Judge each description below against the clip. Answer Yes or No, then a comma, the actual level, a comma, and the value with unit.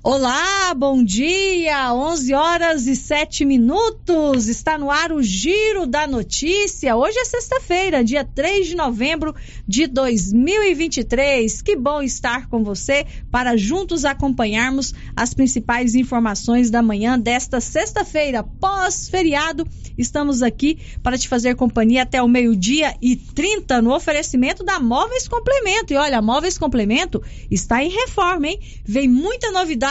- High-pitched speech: Yes, very high, 280 Hz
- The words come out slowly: No, average, 135 wpm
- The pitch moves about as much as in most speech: No, wide, 5.7 semitones